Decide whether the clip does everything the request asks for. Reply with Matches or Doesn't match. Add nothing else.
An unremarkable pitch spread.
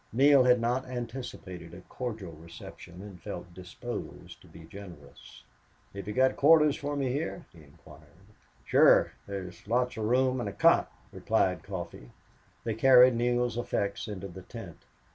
Doesn't match